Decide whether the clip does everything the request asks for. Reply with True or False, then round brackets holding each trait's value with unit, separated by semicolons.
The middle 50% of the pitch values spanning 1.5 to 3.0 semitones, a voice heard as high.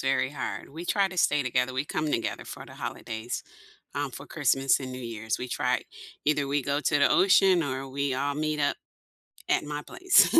False (2.7 semitones; 140 Hz)